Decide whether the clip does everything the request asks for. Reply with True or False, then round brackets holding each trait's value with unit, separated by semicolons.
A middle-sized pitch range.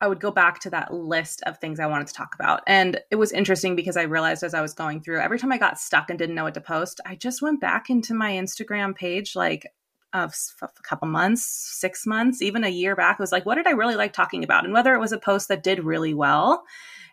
True (4.6 semitones)